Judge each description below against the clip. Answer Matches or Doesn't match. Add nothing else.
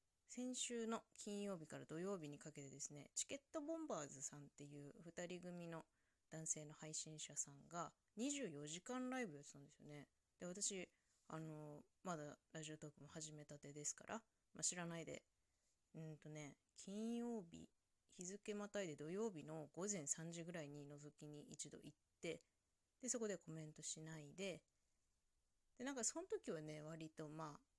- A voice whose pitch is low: Doesn't match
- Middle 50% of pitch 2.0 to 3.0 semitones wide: Doesn't match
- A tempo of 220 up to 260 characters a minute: Doesn't match